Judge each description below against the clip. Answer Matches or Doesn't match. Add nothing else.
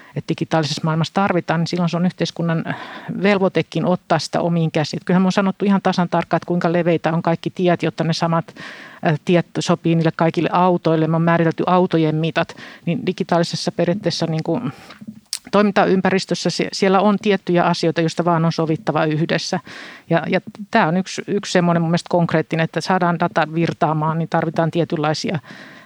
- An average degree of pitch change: Doesn't match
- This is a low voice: Doesn't match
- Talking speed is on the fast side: Matches